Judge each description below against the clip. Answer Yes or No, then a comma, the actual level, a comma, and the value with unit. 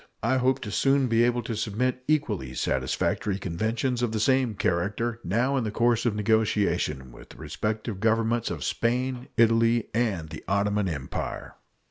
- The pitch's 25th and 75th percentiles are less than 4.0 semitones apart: Yes, average, 3.0 semitones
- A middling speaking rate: Yes, average, 160 wpm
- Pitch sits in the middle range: No, low, 115 Hz